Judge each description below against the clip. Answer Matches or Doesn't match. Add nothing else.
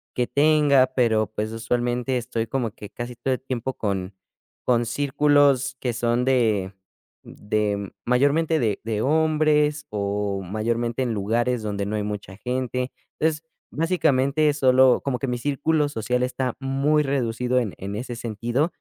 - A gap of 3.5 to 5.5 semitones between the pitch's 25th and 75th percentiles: Matches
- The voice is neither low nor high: Doesn't match